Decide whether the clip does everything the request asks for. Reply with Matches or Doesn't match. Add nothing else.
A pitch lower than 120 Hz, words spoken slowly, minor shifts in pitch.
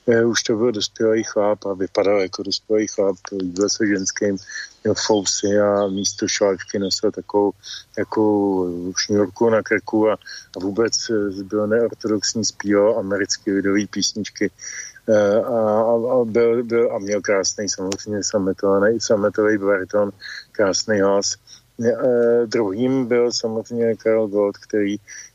Matches